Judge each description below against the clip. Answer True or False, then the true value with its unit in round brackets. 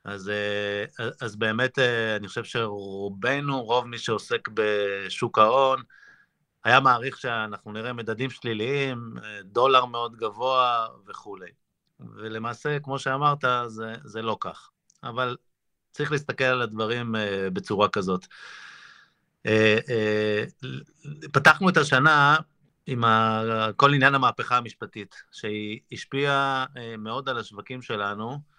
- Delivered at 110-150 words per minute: False (100 wpm)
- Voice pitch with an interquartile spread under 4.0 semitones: True (3.4 semitones)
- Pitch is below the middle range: True (120 Hz)